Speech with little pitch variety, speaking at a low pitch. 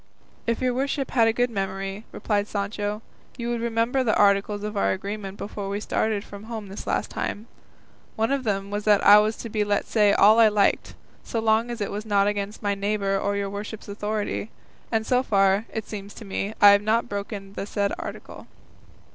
No: narrow, 1.8 semitones; high, 210 Hz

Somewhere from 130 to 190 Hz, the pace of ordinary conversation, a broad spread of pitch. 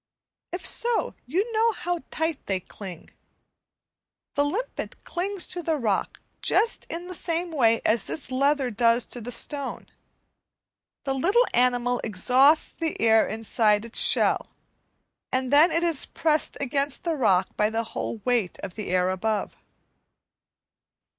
No: very high, 260 Hz; average, 145 wpm; wide, 6.8 semitones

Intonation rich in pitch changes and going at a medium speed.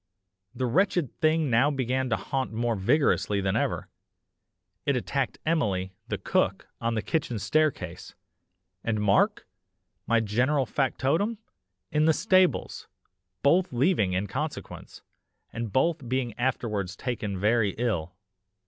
No: wide, 5.8 semitones; slow, 125 wpm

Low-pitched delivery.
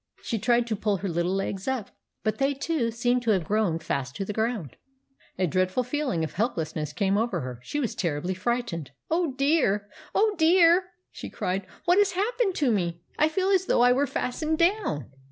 No: high, 230 Hz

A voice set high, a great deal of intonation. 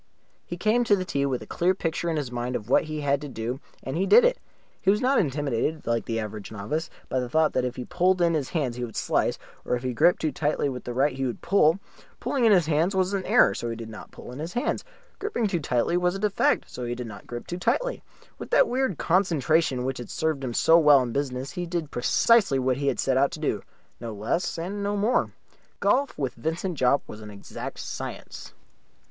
No: medium, 150 Hz; wide, 6.3 semitones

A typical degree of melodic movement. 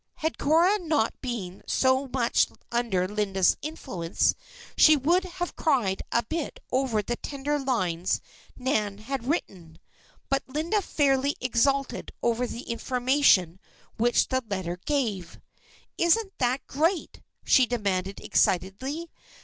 No: wide, 6.0 semitones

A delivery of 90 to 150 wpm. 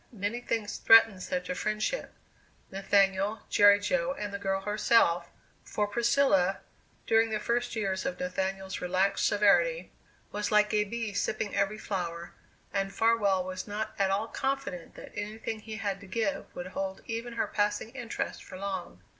No: average, 160 wpm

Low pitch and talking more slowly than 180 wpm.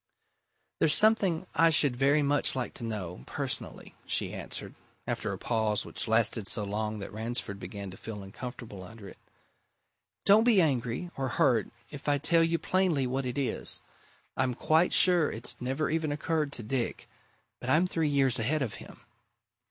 Yes: low, 130 Hz; average, 170 wpm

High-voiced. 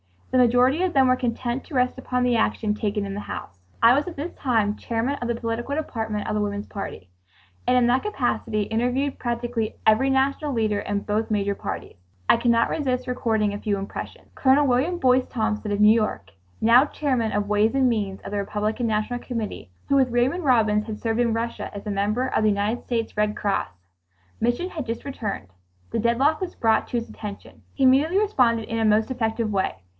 Yes: high, 230 Hz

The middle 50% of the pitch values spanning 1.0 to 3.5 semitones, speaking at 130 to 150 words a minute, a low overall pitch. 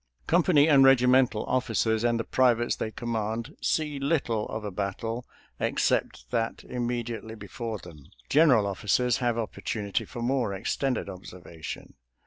Yes: average, 3.2 semitones; slow, 135 wpm; low, 115 Hz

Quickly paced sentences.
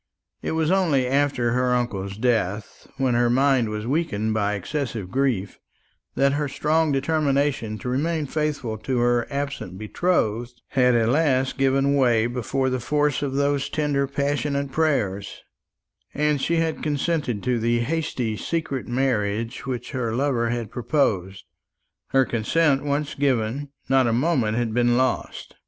No: average, 145 wpm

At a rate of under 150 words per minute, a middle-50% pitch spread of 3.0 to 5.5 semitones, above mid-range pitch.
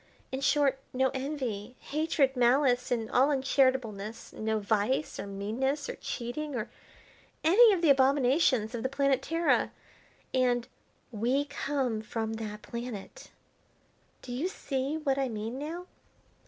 Yes: slow, 135 wpm; average, 3.8 semitones; very high, 260 Hz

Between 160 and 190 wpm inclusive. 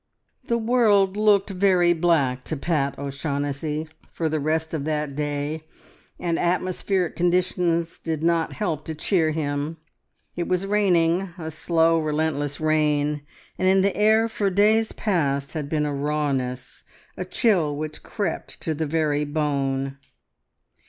No: average, 140 wpm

